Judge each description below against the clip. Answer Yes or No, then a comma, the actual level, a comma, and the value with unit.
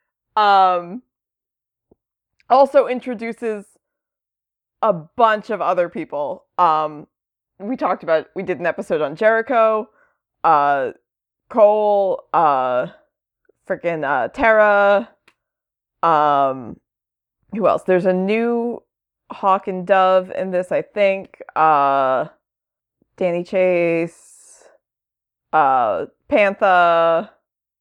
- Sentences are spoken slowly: Yes, slow, 95 wpm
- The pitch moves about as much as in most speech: Yes, average, 4.6 semitones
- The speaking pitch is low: No, high, 195 Hz